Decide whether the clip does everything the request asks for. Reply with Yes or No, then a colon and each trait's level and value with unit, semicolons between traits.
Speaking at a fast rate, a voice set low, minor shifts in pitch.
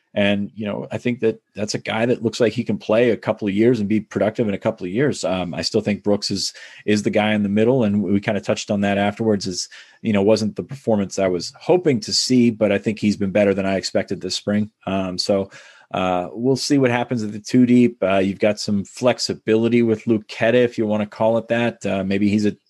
Yes: fast, 260 wpm; low, 105 Hz; narrow, 2.2 semitones